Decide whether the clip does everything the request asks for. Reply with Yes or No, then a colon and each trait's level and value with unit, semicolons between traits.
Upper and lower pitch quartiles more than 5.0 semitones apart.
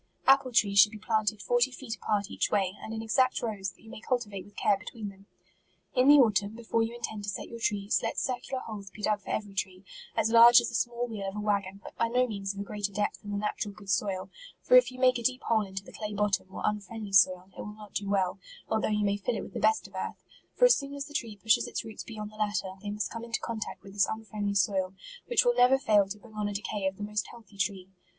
No: narrow, 2.5 semitones